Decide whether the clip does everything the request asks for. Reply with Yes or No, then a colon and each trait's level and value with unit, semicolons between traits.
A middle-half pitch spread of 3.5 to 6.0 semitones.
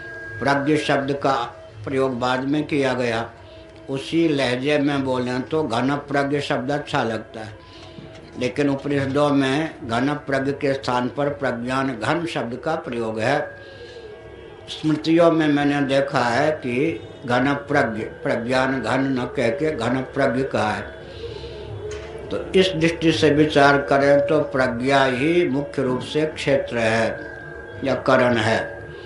No: average, 2.7 semitones